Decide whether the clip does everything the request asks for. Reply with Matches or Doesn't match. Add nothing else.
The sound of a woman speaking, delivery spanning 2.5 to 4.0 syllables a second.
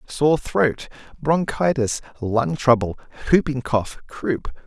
Doesn't match